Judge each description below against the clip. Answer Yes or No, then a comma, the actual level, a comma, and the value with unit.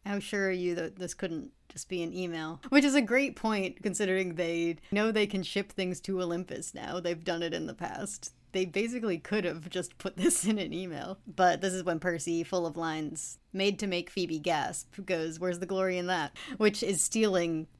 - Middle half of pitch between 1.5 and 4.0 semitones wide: Yes, average, 2.7 semitones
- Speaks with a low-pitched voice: No, medium, 185 Hz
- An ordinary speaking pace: No, fast, 215 wpm